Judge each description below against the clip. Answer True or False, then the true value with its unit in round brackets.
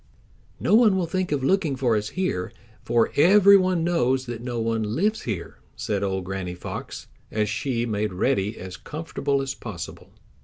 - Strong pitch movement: True (8.1 semitones)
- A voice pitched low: True (125 Hz)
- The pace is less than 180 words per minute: True (170 wpm)